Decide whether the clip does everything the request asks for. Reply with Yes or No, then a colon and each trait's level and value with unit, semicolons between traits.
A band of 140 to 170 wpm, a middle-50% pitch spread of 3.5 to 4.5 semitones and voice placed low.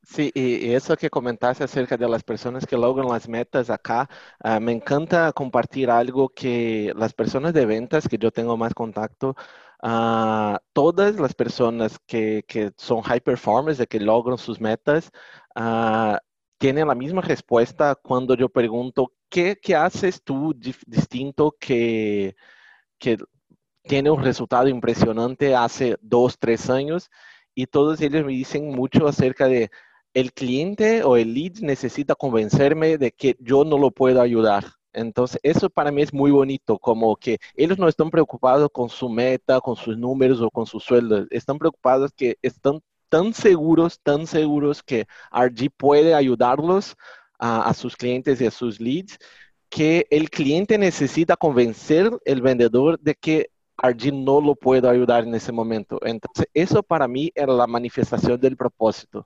Yes: average, 160 wpm; average, 3.9 semitones; low, 130 Hz